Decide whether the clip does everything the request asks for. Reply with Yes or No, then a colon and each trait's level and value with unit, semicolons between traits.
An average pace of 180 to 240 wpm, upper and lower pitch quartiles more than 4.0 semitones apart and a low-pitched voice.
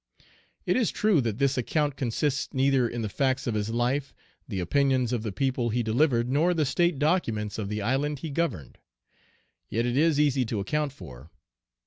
Yes: average, 185 wpm; average, 4.5 semitones; low, 130 Hz